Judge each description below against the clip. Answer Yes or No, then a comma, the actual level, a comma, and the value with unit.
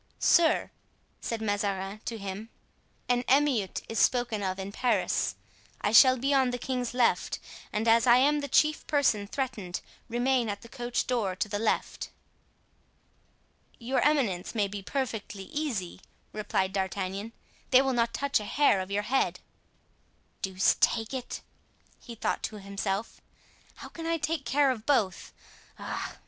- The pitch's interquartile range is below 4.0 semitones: No, average, 4.6 semitones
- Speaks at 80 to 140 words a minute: No, average, 155 wpm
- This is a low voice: No, high, 230 Hz